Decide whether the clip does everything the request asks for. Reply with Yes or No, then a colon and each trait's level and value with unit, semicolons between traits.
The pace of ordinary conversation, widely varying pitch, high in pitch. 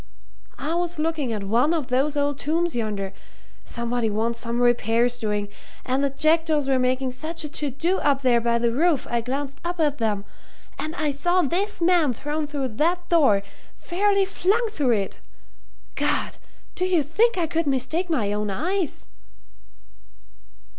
Yes: average, 165 wpm; wide, 5.8 semitones; very high, 285 Hz